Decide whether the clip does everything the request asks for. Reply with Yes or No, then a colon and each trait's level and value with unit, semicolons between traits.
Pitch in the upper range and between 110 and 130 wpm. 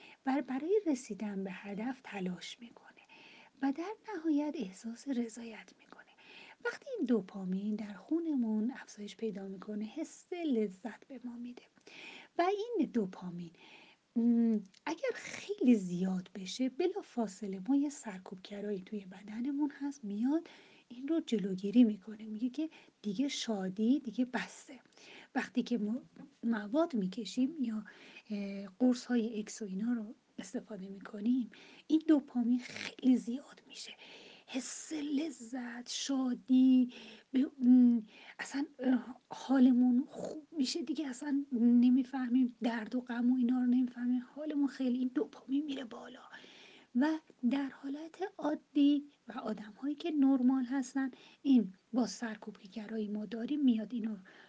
Yes: high, 245 Hz; average, 120 wpm